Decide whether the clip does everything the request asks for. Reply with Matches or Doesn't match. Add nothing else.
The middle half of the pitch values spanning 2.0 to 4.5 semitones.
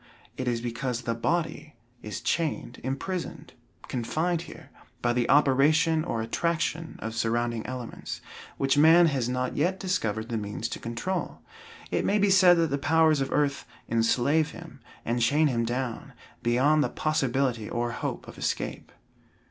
Doesn't match